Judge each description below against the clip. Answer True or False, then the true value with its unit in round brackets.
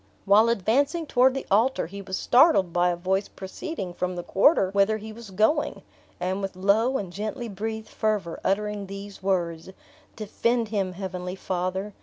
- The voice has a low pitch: False (200 Hz)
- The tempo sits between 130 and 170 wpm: True (165 wpm)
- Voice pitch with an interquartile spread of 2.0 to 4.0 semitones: True (2.9 semitones)